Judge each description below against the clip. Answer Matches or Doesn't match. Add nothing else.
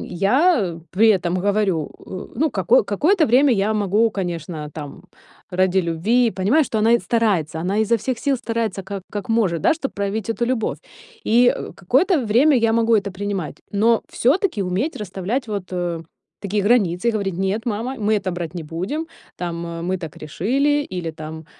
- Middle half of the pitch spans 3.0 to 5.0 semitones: Matches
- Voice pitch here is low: Doesn't match